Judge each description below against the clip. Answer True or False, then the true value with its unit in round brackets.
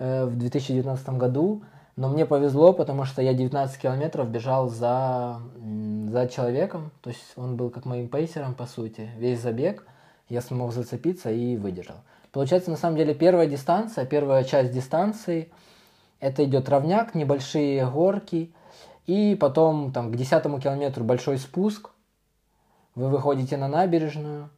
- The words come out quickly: False (140 wpm)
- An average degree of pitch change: True (4.2 semitones)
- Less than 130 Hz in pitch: False (135 Hz)